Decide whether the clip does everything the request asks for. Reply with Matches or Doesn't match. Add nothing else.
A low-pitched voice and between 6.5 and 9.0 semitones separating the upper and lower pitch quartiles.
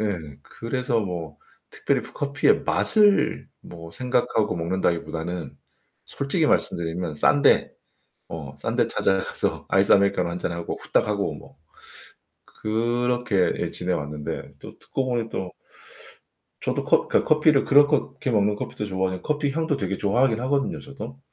Matches